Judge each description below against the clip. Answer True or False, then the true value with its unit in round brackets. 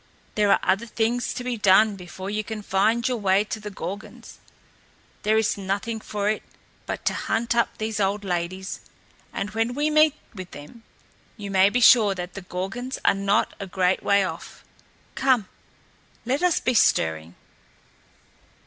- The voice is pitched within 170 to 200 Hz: False (210 Hz)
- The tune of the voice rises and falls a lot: False (3.2 semitones)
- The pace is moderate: True (165 wpm)